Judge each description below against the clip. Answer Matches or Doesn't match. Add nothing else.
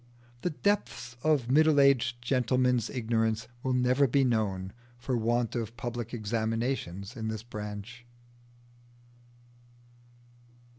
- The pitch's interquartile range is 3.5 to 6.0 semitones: Doesn't match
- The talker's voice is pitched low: Matches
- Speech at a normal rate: Doesn't match